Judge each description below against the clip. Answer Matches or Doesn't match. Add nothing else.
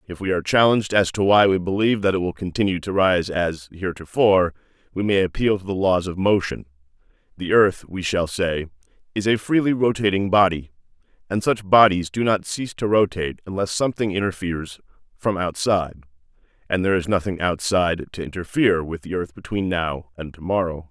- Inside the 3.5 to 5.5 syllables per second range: Doesn't match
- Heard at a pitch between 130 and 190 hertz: Doesn't match